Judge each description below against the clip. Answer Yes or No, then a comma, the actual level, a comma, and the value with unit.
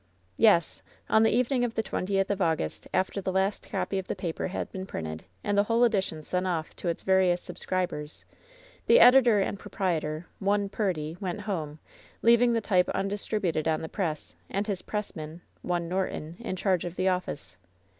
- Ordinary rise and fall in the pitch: Yes, average, 3.4 semitones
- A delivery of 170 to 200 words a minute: Yes, average, 180 wpm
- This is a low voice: No, high, 190 Hz